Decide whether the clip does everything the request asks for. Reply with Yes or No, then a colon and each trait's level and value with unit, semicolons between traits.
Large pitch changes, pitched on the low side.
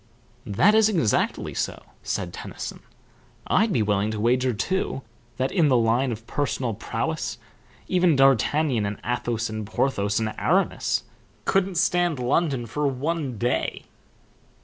Yes: wide, 6.0 semitones; low, 130 Hz